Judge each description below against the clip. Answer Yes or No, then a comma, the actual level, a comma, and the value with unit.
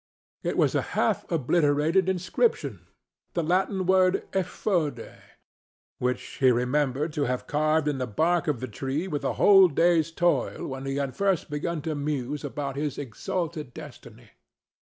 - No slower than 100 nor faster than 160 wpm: Yes, average, 145 wpm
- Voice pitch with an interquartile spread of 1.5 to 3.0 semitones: No, average, 4.3 semitones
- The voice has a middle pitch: Yes, medium, 150 Hz